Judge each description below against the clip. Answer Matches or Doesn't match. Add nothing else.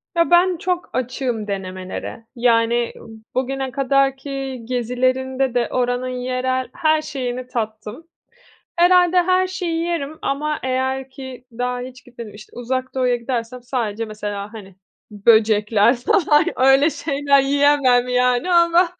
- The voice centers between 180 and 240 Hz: Doesn't match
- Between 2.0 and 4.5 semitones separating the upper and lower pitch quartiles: Matches